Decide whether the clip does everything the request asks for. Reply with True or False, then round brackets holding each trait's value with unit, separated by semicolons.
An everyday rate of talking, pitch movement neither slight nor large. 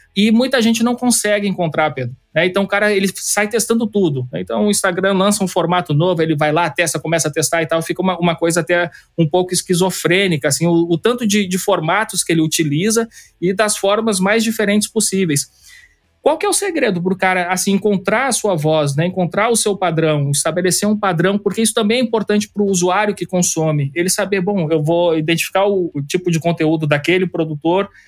False (200 wpm; 3.8 semitones)